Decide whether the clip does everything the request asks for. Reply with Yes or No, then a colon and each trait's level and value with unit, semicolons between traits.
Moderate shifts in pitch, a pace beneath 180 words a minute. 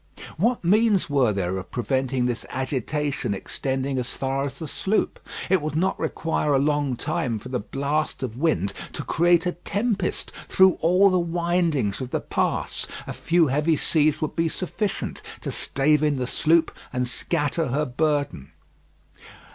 Yes: average, 4.4 semitones; average, 165 wpm